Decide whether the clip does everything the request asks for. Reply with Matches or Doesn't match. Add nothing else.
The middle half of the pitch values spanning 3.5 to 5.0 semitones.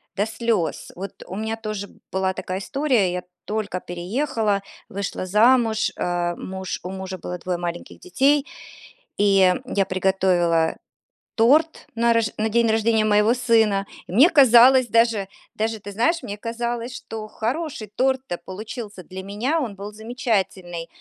Matches